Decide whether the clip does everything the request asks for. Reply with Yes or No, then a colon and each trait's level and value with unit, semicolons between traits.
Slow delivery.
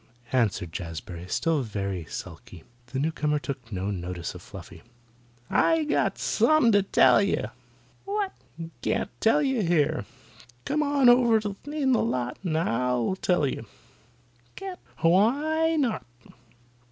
Yes: slow, 130 wpm